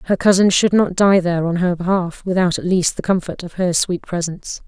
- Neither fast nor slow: No, fast, 230 wpm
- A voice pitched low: No, medium, 180 Hz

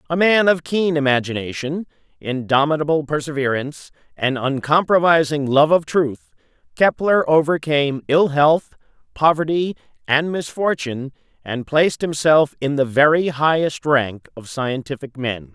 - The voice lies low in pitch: No, medium, 150 Hz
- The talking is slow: Yes, slow, 115 wpm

